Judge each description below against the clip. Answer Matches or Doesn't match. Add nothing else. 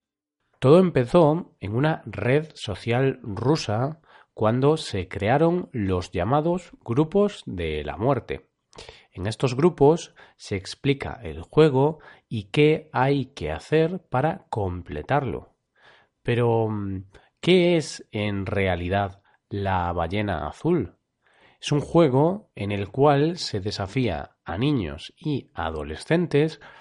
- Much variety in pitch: Matches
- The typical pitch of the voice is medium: Doesn't match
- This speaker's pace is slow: Matches